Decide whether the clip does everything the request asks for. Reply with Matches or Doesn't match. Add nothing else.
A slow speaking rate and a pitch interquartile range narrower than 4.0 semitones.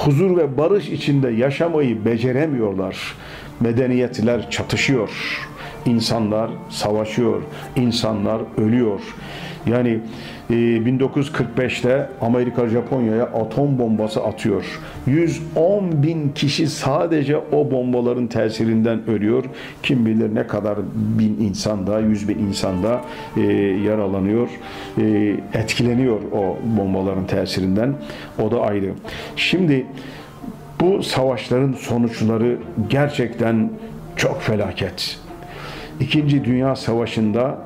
Matches